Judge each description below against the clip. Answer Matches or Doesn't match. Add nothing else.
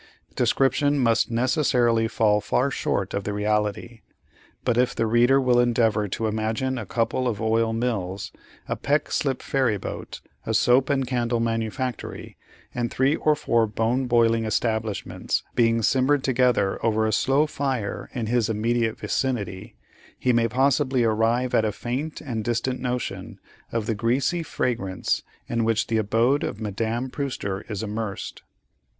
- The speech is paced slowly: Doesn't match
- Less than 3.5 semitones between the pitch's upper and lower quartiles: Matches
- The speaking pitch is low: Matches